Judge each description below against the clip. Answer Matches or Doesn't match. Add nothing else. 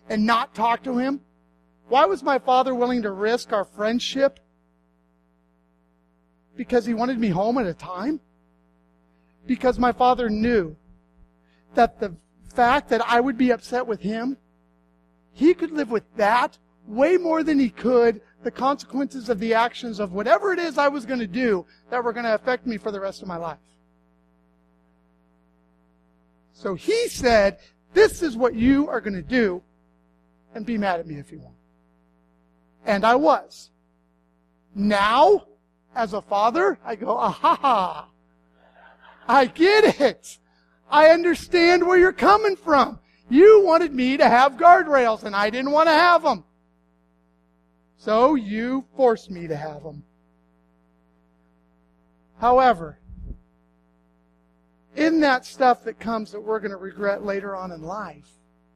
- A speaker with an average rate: Matches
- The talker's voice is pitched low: Doesn't match